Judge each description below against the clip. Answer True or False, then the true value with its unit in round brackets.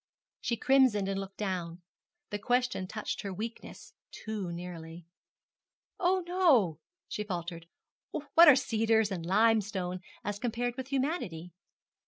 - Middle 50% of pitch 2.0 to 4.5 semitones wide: False (5.4 semitones)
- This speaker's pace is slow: True (125 wpm)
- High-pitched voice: True (210 Hz)